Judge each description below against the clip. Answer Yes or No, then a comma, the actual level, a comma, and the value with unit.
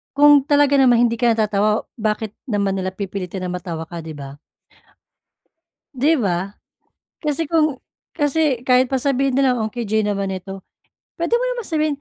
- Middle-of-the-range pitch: No, high, 230 Hz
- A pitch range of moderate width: No, wide, 6.2 semitones